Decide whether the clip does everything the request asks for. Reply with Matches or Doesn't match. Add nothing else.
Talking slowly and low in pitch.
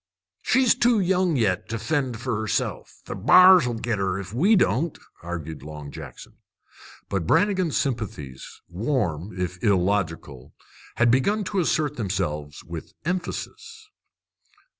Matches